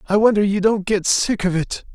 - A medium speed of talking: No, fast, 245 wpm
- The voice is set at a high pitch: Yes, high, 200 Hz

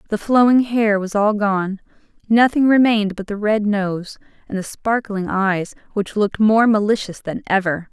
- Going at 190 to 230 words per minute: No, average, 165 wpm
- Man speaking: No, female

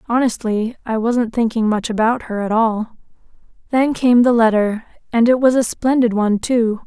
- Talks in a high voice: Yes, high, 230 Hz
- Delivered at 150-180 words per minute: Yes, average, 165 wpm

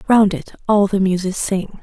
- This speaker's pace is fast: No, average, 195 wpm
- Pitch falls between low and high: No, high, 195 Hz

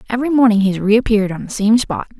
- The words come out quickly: Yes, fast, 245 wpm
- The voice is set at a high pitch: Yes, high, 220 Hz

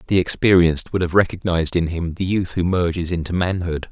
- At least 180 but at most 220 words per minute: Yes, average, 200 wpm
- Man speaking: Yes, male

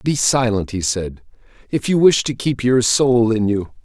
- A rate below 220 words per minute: Yes, fast, 205 wpm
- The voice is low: Yes, low, 115 Hz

